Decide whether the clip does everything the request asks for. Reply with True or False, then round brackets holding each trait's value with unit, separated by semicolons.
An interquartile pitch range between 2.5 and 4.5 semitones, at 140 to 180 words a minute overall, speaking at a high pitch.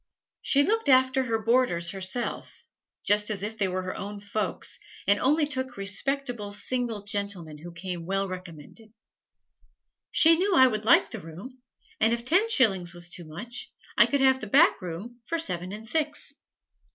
False (5.6 semitones; 170 wpm; 215 Hz)